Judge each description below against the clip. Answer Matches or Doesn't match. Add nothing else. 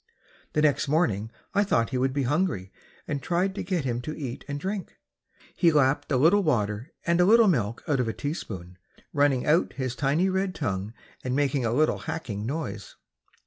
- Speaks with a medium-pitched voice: Matches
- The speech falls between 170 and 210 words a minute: Matches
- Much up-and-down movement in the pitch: Matches